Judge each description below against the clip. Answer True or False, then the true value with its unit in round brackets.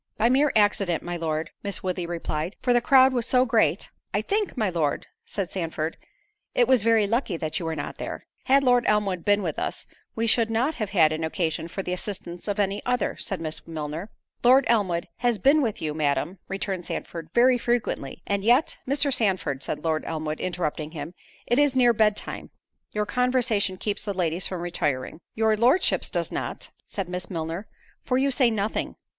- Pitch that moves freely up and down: True (6.2 semitones)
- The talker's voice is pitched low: False (200 Hz)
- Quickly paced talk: False (190 wpm)